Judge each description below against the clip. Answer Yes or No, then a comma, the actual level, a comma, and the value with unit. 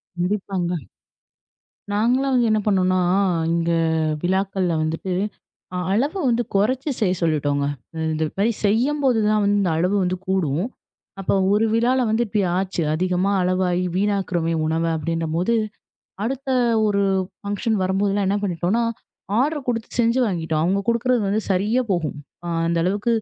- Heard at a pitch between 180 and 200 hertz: Yes, high, 195 Hz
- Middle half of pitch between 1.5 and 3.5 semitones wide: No, average, 4.2 semitones